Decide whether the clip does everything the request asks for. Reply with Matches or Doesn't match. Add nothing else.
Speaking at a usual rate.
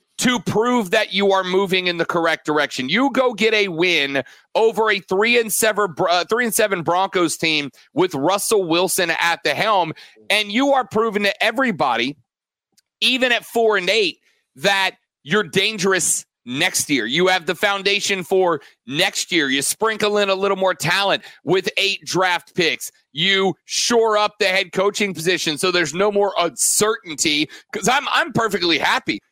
Matches